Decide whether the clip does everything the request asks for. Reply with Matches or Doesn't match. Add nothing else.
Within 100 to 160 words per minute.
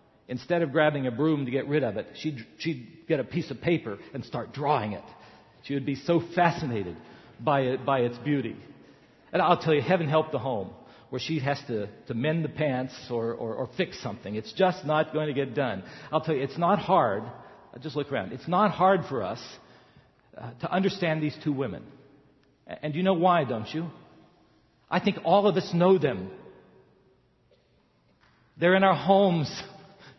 Doesn't match